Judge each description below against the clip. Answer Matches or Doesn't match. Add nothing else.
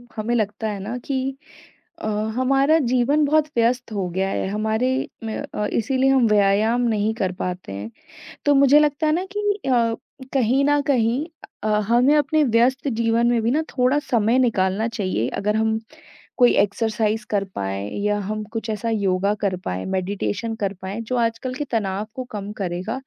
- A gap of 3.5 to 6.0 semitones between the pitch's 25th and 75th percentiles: Matches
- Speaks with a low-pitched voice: Doesn't match